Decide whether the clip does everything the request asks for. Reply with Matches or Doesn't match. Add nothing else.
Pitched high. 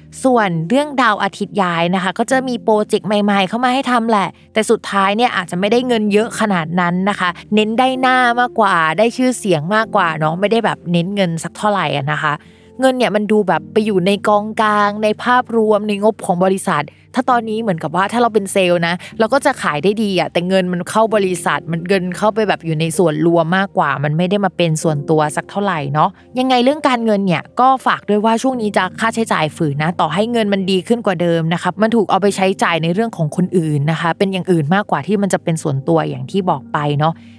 Matches